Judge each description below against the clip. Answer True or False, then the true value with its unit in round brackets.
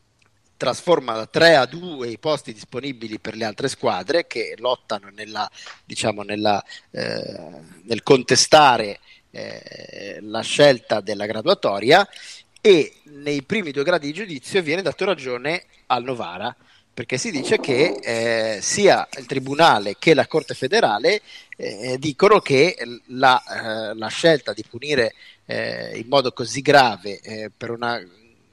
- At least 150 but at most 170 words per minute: False (140 wpm)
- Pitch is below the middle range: True (130 Hz)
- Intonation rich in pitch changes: True (5.8 semitones)